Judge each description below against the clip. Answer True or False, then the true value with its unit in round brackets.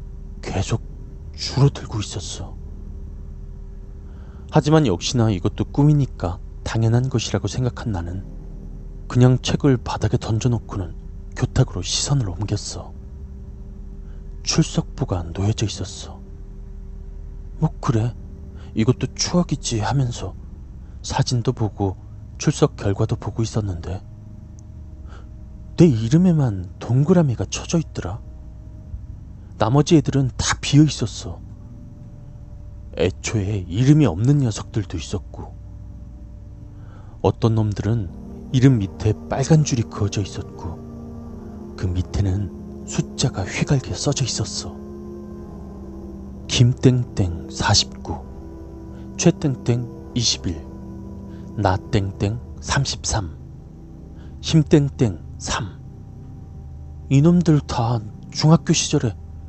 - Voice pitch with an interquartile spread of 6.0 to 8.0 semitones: True (6.5 semitones)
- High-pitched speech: False (100 Hz)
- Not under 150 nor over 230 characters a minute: True (195 characters per minute)